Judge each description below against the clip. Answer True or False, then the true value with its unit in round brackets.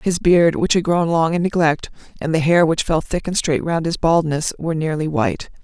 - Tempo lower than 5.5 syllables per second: True (5.3 syllables/s)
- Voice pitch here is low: False (165 Hz)